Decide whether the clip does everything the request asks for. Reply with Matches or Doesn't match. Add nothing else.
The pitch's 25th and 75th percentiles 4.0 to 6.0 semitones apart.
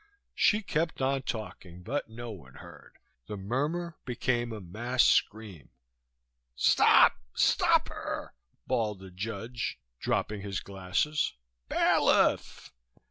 Matches